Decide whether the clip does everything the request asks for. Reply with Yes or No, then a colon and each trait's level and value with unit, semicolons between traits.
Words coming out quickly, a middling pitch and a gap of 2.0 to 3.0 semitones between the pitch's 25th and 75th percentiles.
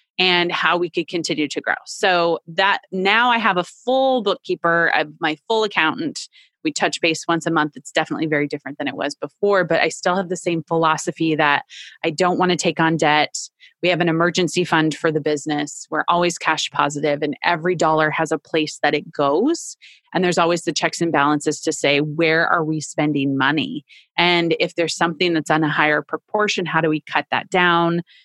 Yes: fast, 210 wpm; medium, 170 Hz; narrow, 2.6 semitones